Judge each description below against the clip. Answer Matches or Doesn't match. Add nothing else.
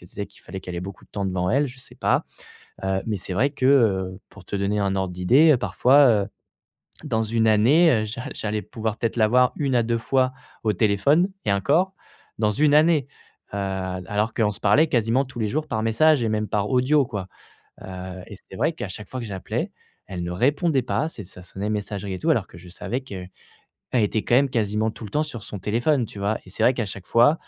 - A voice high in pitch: Doesn't match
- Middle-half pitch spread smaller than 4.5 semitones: Doesn't match